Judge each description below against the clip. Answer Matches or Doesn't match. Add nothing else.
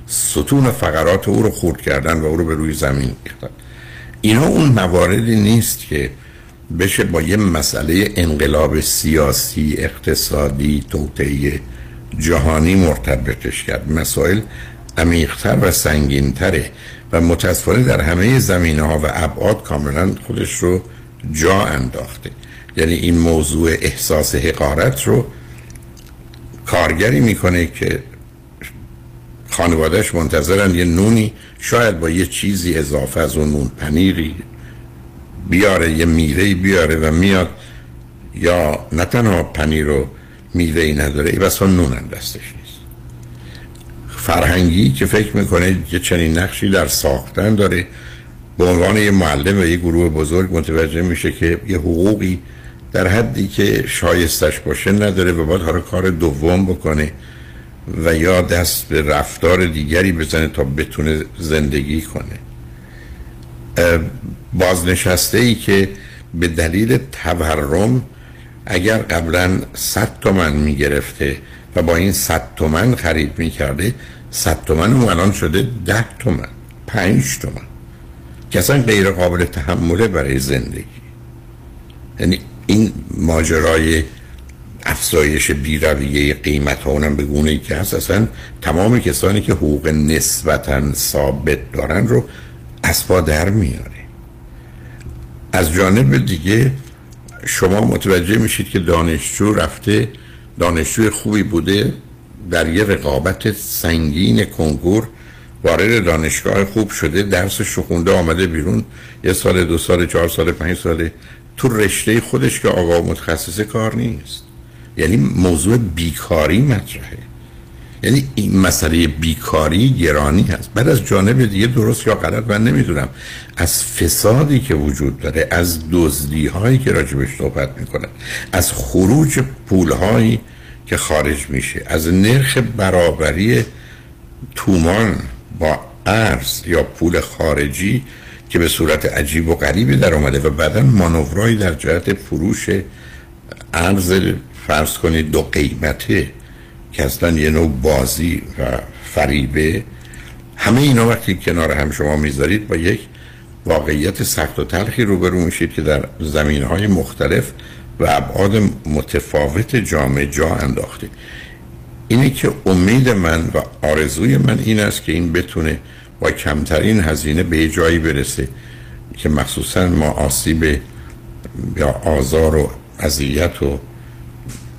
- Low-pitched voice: Matches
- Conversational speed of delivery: Matches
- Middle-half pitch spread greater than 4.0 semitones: Matches